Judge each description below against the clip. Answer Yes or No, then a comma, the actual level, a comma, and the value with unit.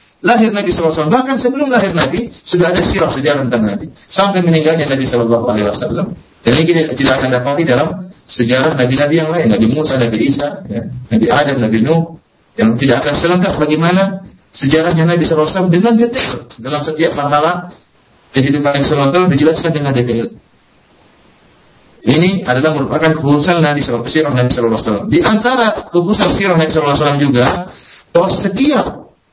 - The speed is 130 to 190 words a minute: Yes, fast, 155 wpm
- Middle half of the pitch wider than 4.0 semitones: Yes, average, 5.2 semitones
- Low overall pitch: No, medium, 155 Hz